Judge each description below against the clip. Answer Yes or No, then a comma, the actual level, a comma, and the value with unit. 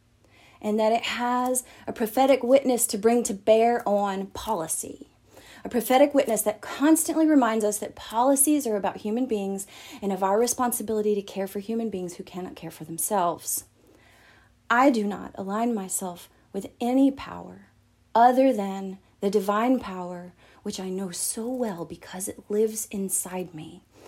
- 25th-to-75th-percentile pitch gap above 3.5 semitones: Yes, average, 4.2 semitones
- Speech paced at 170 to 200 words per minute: No, average, 155 wpm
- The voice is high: Yes, high, 210 Hz